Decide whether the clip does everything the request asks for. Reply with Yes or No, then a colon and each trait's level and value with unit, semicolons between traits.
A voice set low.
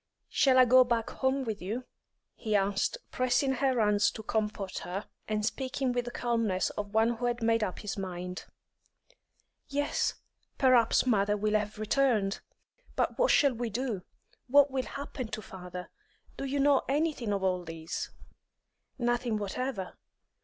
No: high, 230 Hz